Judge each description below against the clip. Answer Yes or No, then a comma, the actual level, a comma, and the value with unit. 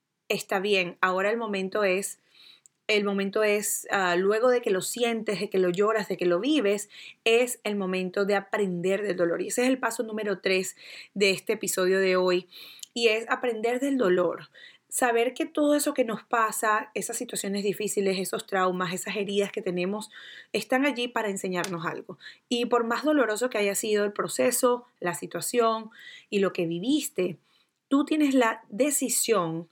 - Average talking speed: Yes, average, 175 wpm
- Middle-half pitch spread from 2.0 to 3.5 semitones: No, average, 4.1 semitones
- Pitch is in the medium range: No, high, 210 Hz